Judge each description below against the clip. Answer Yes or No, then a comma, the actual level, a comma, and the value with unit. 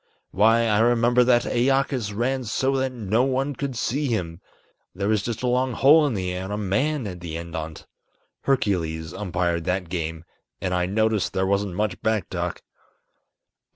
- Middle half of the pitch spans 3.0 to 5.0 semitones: No, wide, 5.5 semitones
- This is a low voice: Yes, low, 105 Hz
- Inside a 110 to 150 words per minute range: No, average, 180 wpm